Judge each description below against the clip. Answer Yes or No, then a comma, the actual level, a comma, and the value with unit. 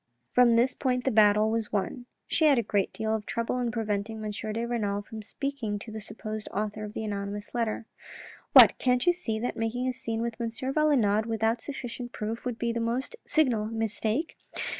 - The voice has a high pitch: Yes, high, 225 Hz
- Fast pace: Yes, fast, 210 wpm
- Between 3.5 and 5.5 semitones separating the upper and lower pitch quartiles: No, narrow, 2.4 semitones